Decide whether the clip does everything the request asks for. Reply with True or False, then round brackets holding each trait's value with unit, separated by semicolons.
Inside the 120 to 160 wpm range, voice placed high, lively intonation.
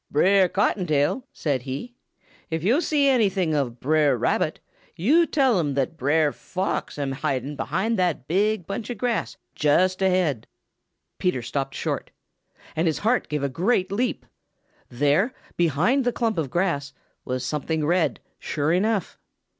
False (145 wpm; 170 Hz; 6.2 semitones)